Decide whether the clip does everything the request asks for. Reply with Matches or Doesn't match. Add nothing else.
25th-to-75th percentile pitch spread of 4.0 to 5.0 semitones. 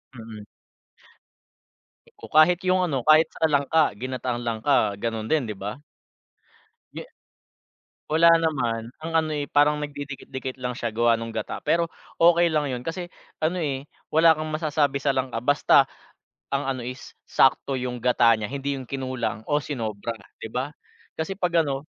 Matches